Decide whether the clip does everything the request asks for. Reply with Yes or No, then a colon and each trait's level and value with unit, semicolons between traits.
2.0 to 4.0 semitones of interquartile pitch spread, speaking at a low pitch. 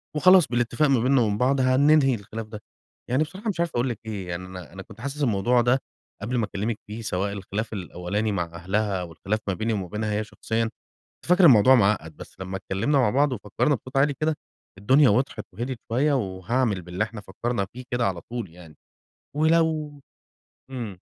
No: average, 5.2 semitones; low, 115 Hz